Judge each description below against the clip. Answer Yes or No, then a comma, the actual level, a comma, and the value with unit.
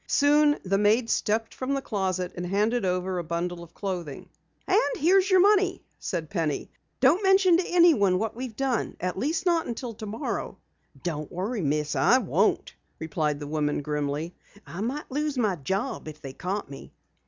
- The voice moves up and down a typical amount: No, wide, 8.2 semitones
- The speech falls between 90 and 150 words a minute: No, average, 175 wpm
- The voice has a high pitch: Yes, high, 205 Hz